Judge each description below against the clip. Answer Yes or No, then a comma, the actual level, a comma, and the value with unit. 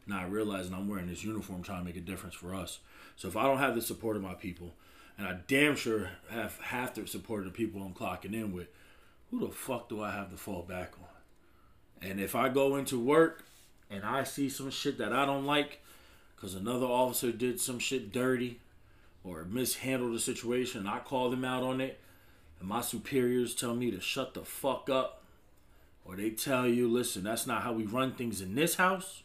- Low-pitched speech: Yes, low, 115 Hz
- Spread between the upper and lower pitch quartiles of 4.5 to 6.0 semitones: Yes, average, 5.1 semitones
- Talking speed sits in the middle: No, fast, 215 wpm